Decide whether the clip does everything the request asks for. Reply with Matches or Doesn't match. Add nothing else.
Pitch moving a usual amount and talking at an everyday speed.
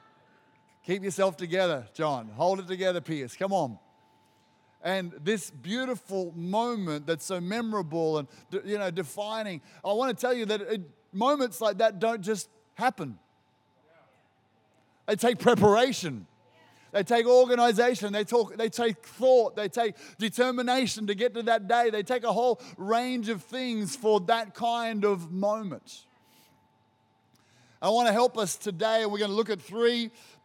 Doesn't match